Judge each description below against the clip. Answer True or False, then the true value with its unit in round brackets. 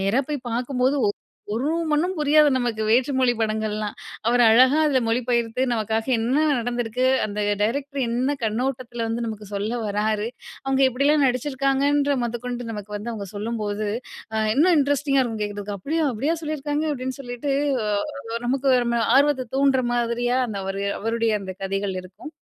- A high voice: True (245 Hz)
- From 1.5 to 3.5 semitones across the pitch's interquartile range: False (3.9 semitones)